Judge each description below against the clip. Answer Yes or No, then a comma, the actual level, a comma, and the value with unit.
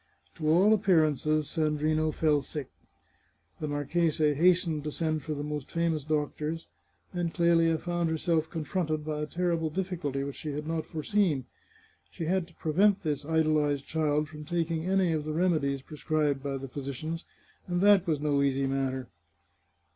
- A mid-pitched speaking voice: Yes, medium, 155 Hz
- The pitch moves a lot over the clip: No, narrow, 2.4 semitones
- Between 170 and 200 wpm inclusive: No, average, 160 wpm